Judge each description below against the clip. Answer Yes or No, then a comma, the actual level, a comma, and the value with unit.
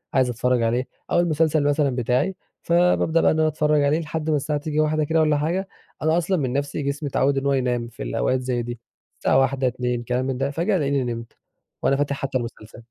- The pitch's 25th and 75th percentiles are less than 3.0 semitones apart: No, average, 3.6 semitones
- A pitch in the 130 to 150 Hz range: Yes, medium, 140 Hz